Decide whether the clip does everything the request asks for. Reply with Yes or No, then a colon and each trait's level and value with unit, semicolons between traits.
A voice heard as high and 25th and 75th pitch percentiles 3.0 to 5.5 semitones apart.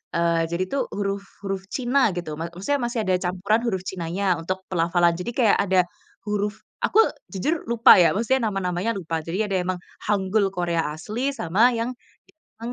Yes: high, 195 Hz; average, 3.7 semitones